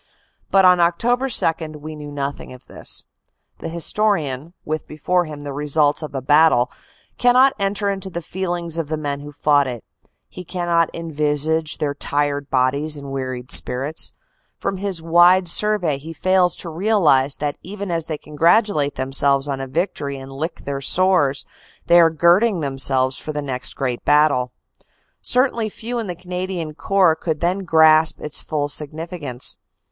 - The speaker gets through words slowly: No, average, 160 wpm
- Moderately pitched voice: Yes, medium, 155 Hz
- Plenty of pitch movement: No, average, 4.0 semitones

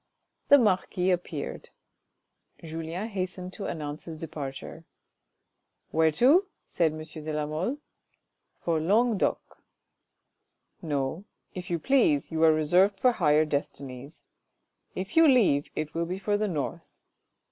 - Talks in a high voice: No, medium, 165 Hz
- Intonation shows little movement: No, average, 4.3 semitones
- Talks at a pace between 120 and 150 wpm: Yes, average, 140 wpm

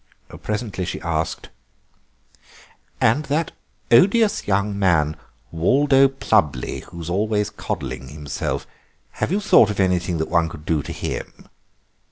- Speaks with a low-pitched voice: Yes, very low, 95 Hz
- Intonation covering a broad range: Yes, wide, 6.4 semitones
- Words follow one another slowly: Yes, slow, 125 wpm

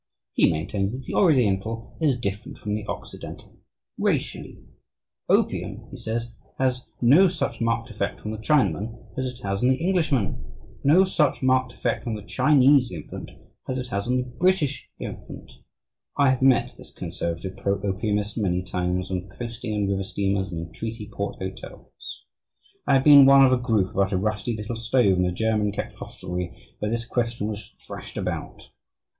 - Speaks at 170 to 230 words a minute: Yes, average, 175 wpm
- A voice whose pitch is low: Yes, low, 115 Hz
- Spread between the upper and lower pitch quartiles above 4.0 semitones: Yes, average, 4.6 semitones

